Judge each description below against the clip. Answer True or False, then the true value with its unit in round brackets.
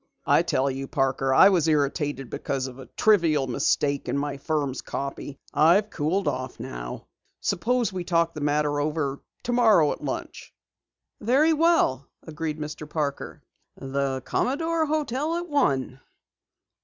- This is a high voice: False (150 Hz)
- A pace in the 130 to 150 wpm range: True (140 wpm)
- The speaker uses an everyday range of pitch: False (7.2 semitones)